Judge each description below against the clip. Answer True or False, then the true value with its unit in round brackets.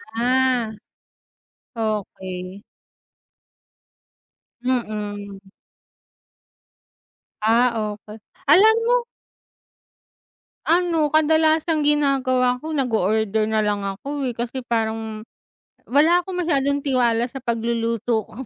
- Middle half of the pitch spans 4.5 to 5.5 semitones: True (5.0 semitones)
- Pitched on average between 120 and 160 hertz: False (245 Hz)